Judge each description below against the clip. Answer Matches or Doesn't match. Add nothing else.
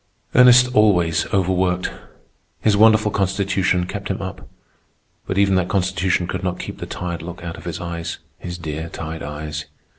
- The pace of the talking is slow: Doesn't match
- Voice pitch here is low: Matches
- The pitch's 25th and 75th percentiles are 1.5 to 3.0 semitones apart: Matches